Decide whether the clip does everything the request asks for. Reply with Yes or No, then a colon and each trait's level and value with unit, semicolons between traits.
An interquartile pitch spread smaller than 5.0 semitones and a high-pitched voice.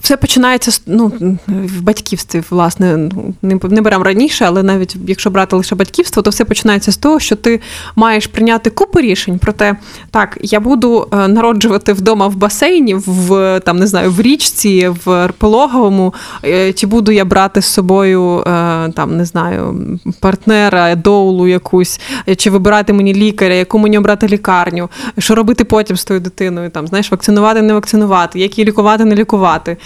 Yes: average, 2.8 semitones; high, 200 Hz